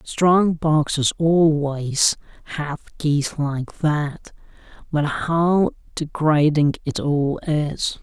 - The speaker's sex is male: Yes, male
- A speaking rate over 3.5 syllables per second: No, 2.7 syllables/s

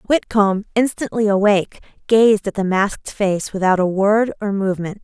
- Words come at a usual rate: Yes, average, 155 wpm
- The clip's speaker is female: Yes, female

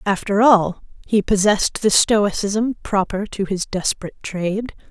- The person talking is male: No, female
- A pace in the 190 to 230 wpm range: No, slow, 135 wpm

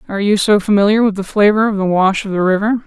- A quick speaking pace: Yes, fast, 270 wpm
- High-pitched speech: Yes, high, 200 Hz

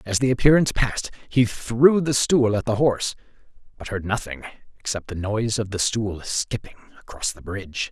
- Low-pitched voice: Yes, low, 115 Hz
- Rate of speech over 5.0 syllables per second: Yes, 5.5 syllables/s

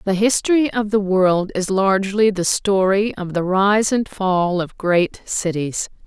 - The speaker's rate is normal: Yes, average, 170 wpm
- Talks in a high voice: Yes, high, 195 Hz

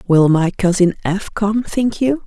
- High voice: Yes, high, 195 Hz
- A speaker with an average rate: Yes, average, 185 wpm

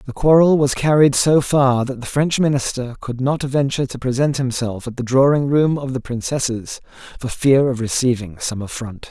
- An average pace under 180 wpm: No, average, 190 wpm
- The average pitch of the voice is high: No, low, 130 Hz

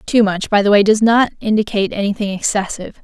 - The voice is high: Yes, high, 205 Hz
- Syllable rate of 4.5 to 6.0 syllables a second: No, 6.4 syllables/s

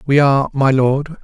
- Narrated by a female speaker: No, male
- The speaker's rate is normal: Yes, average, 195 wpm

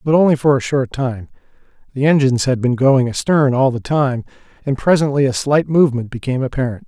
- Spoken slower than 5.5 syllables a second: No, 6.0 syllables/s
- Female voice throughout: No, male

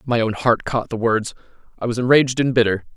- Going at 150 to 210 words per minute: No, fast, 225 wpm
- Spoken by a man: Yes, male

